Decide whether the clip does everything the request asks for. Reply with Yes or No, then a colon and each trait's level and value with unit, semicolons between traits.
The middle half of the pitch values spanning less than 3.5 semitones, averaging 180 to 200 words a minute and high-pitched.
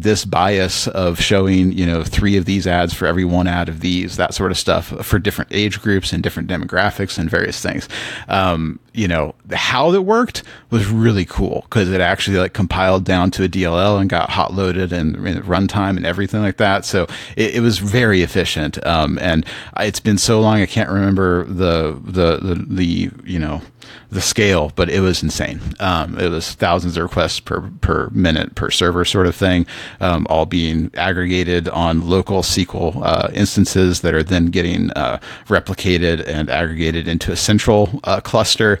No: narrow, 2.4 semitones; average, 190 wpm; very low, 95 Hz